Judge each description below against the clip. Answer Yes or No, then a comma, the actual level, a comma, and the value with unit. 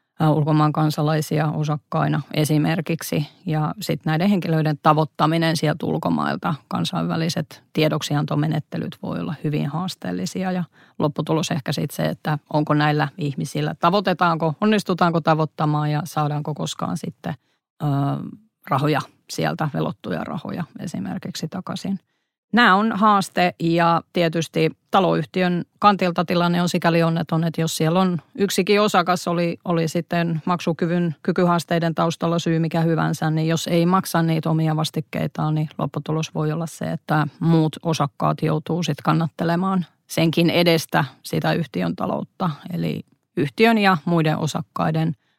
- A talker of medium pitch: Yes, medium, 165 Hz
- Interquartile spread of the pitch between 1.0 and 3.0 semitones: Yes, narrow, 2.4 semitones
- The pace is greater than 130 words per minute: No, average, 125 wpm